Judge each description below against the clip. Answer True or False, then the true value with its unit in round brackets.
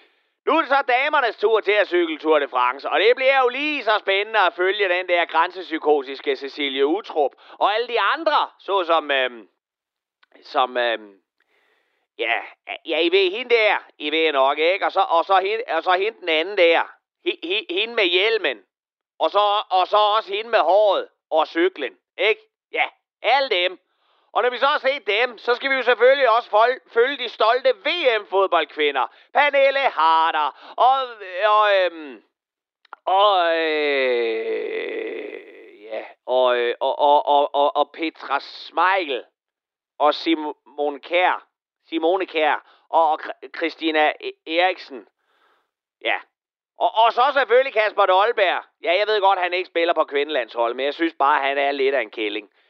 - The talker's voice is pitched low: False (195 Hz)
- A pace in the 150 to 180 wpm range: True (155 wpm)